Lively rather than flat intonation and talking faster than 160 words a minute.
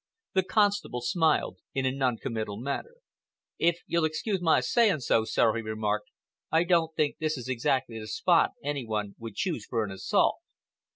Yes: wide, 6.7 semitones; average, 175 wpm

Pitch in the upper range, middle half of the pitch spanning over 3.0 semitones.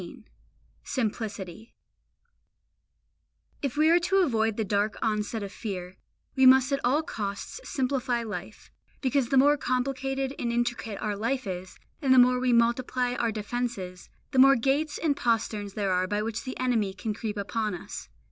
Yes: high, 235 Hz; average, 4.0 semitones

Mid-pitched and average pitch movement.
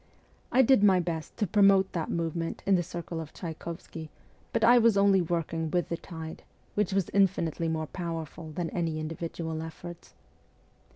Yes: medium, 170 Hz; average, 3.0 semitones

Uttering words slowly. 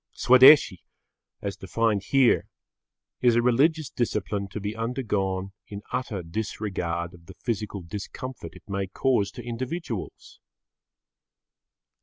Yes: slow, 115 wpm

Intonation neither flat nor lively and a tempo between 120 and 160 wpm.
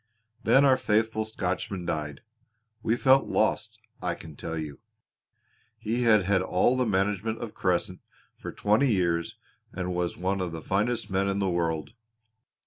Yes: average, 4.0 semitones; average, 155 wpm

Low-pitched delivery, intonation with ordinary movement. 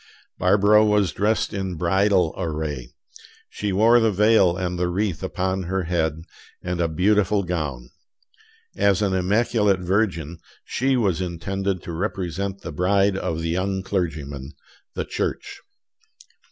Yes: very low, 95 Hz; average, 3.0 semitones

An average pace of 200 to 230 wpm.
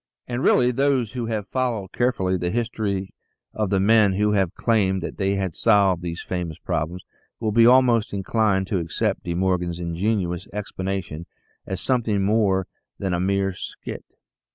No: average, 165 wpm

